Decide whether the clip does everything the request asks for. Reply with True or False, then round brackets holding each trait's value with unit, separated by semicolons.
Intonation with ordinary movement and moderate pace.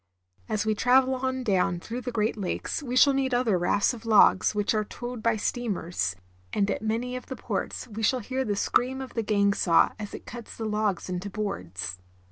False (3.7 semitones; 210 wpm)